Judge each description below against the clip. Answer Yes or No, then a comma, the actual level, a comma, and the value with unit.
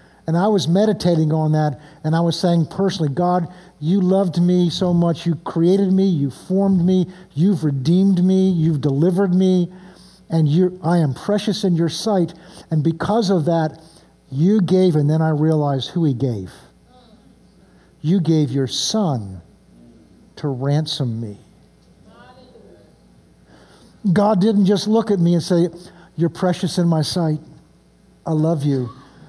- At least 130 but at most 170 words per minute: Yes, average, 150 wpm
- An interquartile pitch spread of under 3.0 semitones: No, average, 3.4 semitones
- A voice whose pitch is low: No, medium, 170 Hz